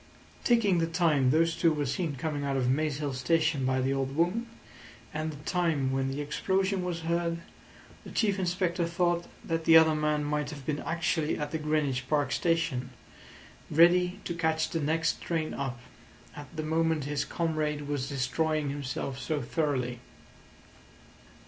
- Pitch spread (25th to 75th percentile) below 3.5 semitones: Yes, average, 2.9 semitones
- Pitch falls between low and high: Yes, medium, 155 Hz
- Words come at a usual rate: Yes, average, 165 wpm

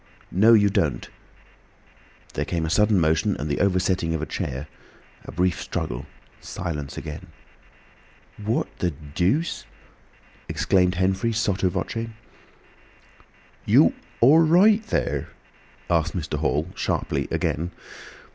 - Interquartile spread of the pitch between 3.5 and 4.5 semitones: No, average, 5.0 semitones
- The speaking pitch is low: Yes, very low, 90 Hz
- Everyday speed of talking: No, slow, 110 wpm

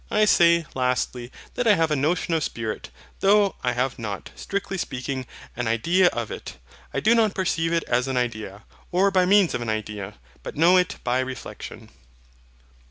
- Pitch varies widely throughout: Yes, wide, 7.2 semitones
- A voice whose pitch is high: No, medium, 140 Hz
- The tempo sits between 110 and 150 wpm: No, average, 180 wpm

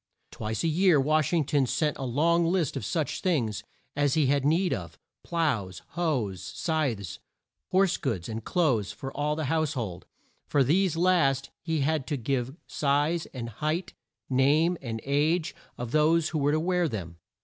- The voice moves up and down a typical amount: Yes, average, 4.3 semitones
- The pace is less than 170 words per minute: No, average, 175 wpm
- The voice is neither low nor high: Yes, medium, 145 Hz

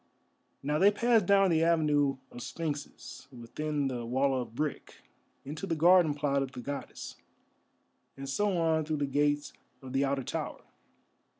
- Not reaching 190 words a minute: Yes, average, 160 wpm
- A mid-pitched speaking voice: Yes, medium, 145 Hz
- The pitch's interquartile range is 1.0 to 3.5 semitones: Yes, average, 3.2 semitones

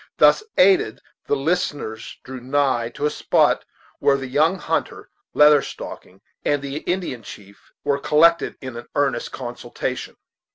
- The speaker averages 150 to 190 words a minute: No, average, 140 wpm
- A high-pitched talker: No, medium, 140 Hz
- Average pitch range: Yes, average, 3.5 semitones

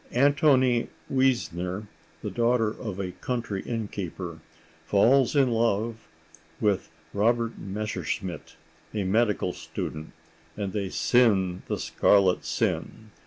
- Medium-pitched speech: No, low, 110 Hz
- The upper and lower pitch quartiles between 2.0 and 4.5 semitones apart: Yes, average, 3.8 semitones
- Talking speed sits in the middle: No, slow, 105 wpm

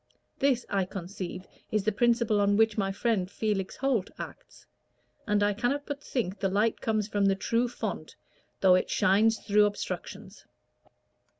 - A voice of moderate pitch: No, high, 210 Hz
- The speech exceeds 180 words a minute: No, average, 160 wpm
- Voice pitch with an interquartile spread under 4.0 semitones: Yes, average, 2.8 semitones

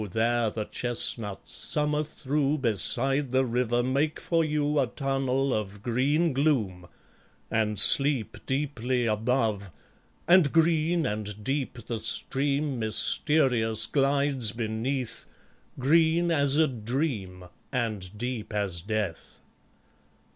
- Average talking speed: No, slow, 110 wpm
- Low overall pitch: Yes, low, 125 Hz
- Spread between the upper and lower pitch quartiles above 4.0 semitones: Yes, average, 4.7 semitones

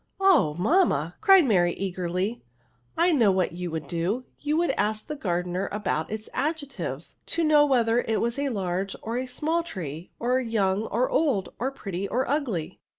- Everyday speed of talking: Yes, average, 185 wpm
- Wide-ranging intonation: Yes, wide, 7.6 semitones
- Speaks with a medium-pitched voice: No, high, 220 Hz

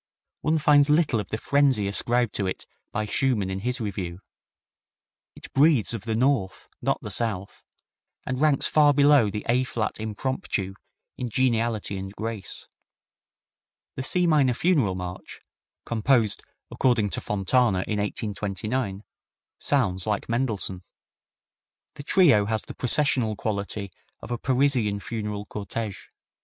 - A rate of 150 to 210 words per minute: No, slow, 135 wpm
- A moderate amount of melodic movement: Yes, average, 4.5 semitones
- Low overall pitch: Yes, low, 115 Hz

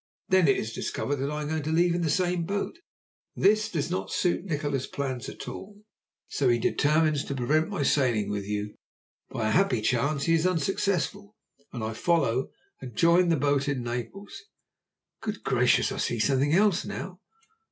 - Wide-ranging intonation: Yes, wide, 5.9 semitones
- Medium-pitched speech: Yes, medium, 150 Hz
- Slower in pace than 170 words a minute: No, average, 185 wpm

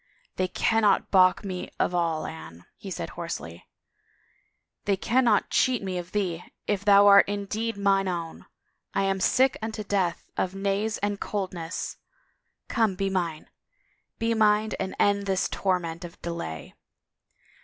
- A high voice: Yes, high, 195 Hz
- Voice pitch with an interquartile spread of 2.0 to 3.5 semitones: Yes, average, 2.8 semitones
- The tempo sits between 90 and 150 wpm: Yes, average, 145 wpm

